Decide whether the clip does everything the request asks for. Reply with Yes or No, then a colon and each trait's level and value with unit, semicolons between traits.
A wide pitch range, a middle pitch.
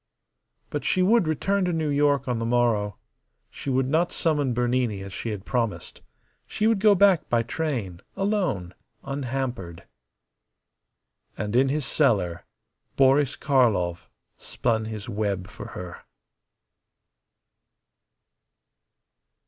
No: wide, 6.4 semitones; low, 125 Hz